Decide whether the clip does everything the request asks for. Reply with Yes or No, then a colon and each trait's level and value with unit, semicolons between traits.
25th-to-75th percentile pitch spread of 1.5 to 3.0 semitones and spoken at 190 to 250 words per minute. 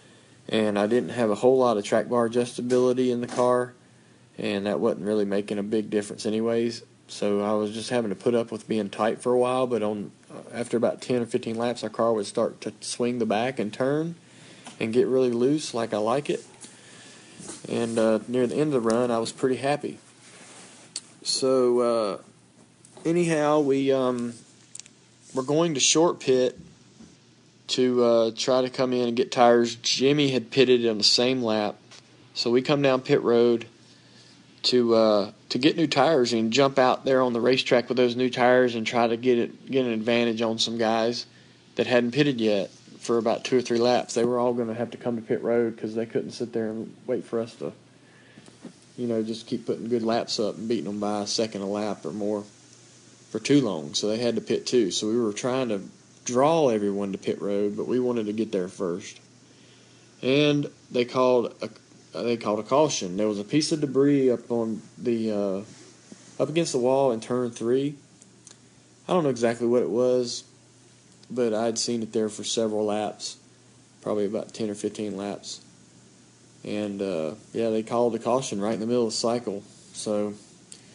Yes: narrow, 2.5 semitones; average, 200 wpm